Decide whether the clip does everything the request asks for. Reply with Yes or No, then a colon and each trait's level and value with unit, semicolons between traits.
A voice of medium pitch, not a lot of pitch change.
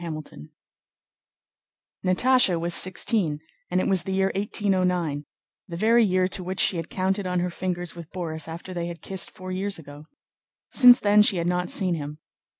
Yes: medium, 180 Hz; narrow, 2.2 semitones